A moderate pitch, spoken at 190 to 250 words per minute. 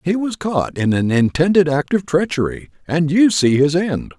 Yes: medium, 160 Hz; average, 200 wpm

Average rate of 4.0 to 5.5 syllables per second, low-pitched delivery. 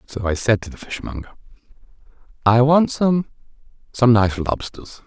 Yes: 4.7 syllables/s; low, 115 Hz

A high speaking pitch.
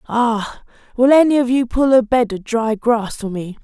Yes: high, 235 Hz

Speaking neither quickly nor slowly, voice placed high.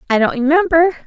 Yes: average, 170 wpm; very high, 300 Hz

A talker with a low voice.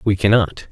Yes: low, 100 Hz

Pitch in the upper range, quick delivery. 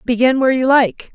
Yes: very high, 250 Hz; fast, 210 wpm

